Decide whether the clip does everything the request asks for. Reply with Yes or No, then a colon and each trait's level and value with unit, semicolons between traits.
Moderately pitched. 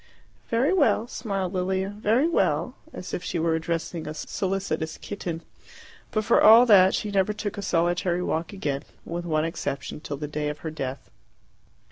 Yes: medium, 180 Hz